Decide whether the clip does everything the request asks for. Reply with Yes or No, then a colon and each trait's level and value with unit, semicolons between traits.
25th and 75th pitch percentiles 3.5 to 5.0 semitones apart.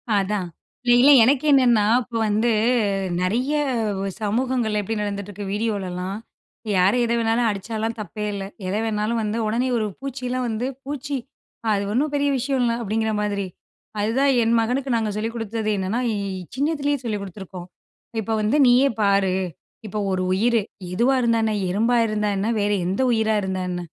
No: average, 3.1 semitones